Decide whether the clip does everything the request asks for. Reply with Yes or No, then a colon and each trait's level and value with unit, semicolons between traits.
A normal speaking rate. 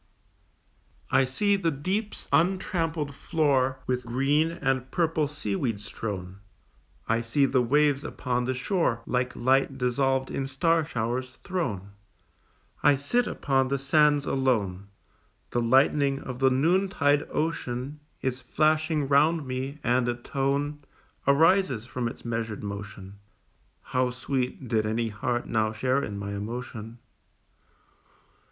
No: slow, 125 wpm